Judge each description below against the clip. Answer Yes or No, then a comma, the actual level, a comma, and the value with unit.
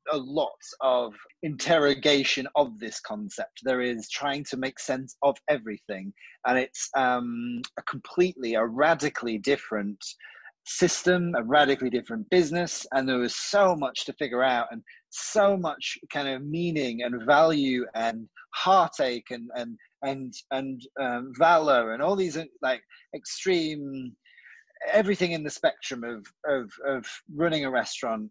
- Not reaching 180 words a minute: Yes, average, 140 wpm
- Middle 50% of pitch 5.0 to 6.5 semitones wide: Yes, wide, 5.5 semitones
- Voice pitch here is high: No, low, 135 Hz